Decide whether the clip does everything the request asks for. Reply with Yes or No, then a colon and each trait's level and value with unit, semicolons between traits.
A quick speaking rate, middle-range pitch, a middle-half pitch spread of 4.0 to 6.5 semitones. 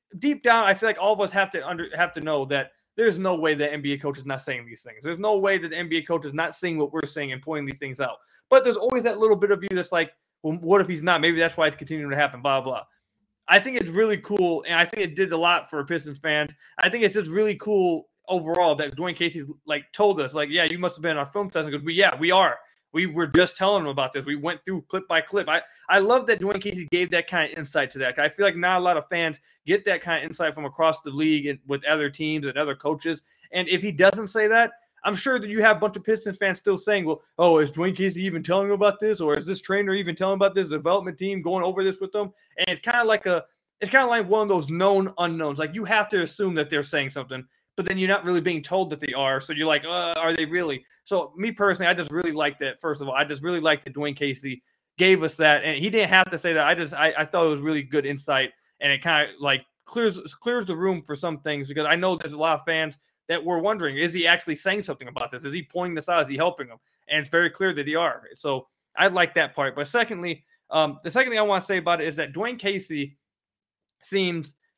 Yes: fast, 285 wpm; medium, 170 Hz; average, 4.3 semitones